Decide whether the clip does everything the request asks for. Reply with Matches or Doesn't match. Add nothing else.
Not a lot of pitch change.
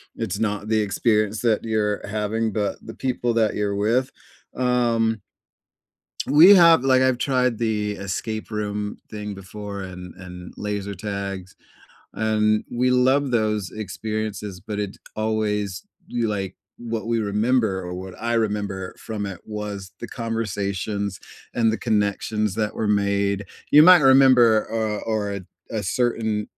Matches